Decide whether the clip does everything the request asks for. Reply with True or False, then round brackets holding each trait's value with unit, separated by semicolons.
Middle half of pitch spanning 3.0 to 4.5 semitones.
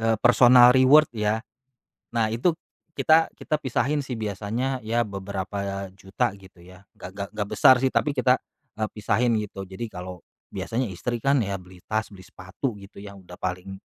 True (4.2 semitones)